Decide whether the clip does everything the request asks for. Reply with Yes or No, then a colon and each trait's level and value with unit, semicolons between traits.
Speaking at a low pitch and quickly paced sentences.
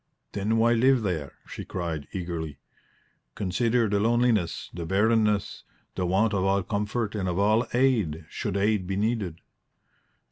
No: low, 100 Hz; average, 145 wpm